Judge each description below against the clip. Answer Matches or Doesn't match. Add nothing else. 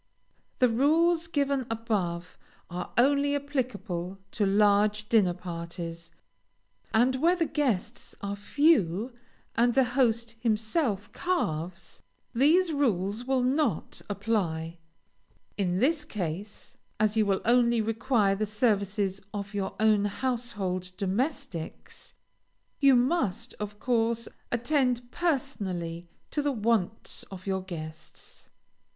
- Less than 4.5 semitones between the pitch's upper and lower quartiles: Doesn't match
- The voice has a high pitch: Matches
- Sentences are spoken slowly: Matches